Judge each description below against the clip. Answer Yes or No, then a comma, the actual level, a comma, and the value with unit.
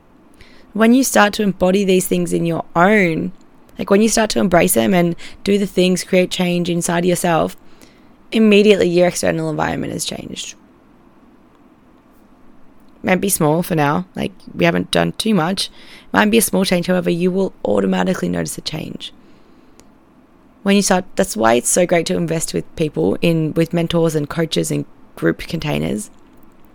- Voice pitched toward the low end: No, medium, 180 Hz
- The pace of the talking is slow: No, average, 170 wpm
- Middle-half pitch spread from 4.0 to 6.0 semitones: No, average, 3.6 semitones